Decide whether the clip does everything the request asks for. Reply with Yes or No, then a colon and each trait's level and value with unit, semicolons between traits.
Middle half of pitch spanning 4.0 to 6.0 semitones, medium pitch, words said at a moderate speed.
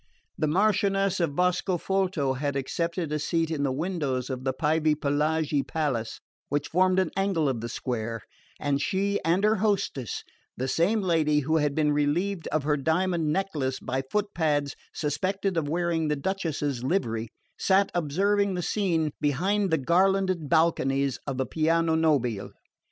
Yes: average, 4.7 semitones; medium, 160 Hz; average, 150 wpm